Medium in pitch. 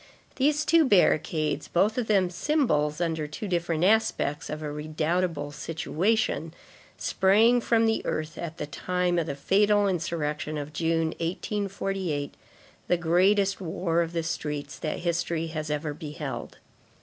Yes: medium, 170 Hz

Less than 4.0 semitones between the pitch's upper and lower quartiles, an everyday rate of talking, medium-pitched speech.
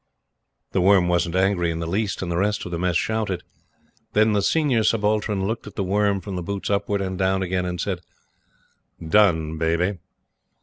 No: average, 2.8 semitones; average, 185 wpm; very low, 95 Hz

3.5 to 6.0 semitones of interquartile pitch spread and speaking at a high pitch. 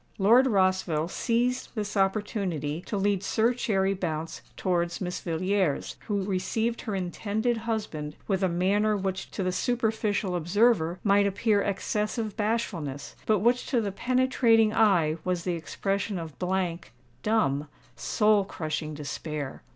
Yes: average, 4.1 semitones; high, 195 Hz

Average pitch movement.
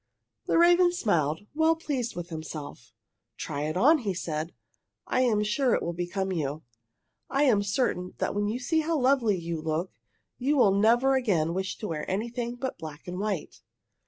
No: wide, 7.3 semitones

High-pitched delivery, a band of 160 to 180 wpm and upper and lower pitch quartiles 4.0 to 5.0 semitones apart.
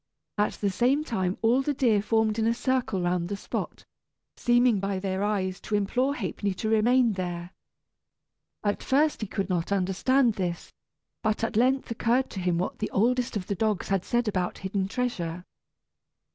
Yes: high, 210 Hz; average, 175 wpm; average, 4.3 semitones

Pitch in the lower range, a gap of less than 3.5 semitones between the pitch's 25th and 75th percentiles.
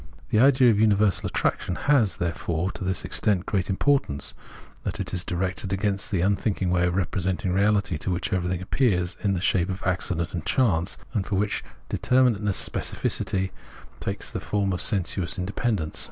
Yes: very low, 95 Hz; average, 2.7 semitones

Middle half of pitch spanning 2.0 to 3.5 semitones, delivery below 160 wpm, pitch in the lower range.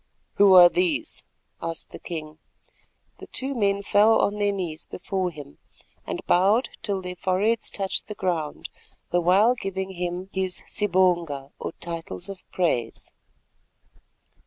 No: average, 2.9 semitones; slow, 135 wpm; medium, 185 Hz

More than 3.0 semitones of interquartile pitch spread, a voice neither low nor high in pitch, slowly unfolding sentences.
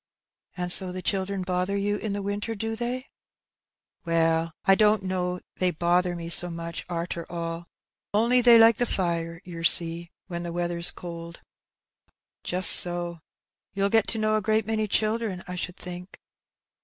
No: average, 3.4 semitones; medium, 180 Hz; average, 170 wpm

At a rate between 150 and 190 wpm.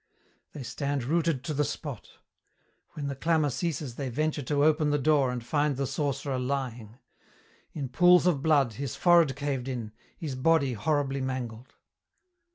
Yes: average, 160 wpm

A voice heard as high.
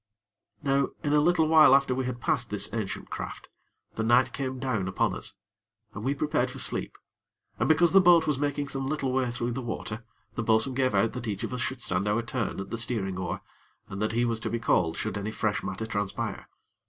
No: low, 120 Hz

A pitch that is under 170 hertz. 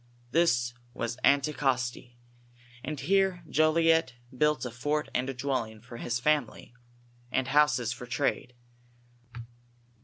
Yes: low, 135 Hz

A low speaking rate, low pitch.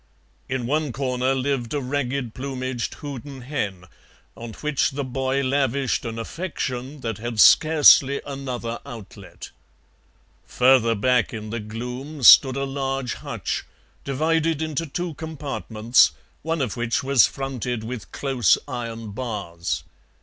Yes: slow, 130 wpm; low, 130 Hz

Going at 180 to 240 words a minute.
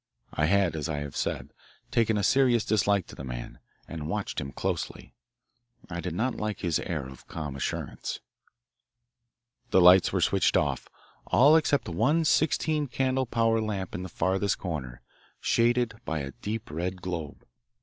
No: average, 160 wpm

